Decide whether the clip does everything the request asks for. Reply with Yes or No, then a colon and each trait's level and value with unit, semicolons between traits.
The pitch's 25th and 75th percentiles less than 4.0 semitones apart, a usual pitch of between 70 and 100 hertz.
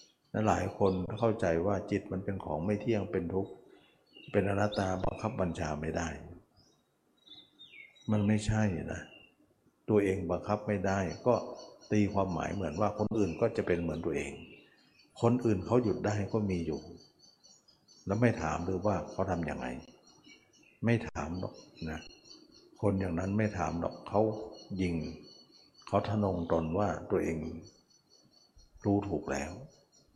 Yes: average, 3.4 semitones; very low, 95 Hz